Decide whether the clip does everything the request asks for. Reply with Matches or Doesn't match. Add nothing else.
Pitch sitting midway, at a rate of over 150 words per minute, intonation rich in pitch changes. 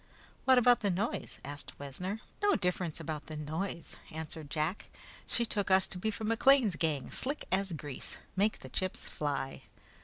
Matches